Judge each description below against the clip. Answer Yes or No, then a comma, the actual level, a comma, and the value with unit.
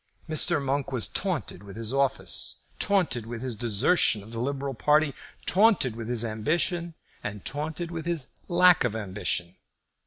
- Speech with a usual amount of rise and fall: No, wide, 6.5 semitones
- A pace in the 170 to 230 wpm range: No, average, 155 wpm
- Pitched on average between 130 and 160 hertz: Yes, low, 135 Hz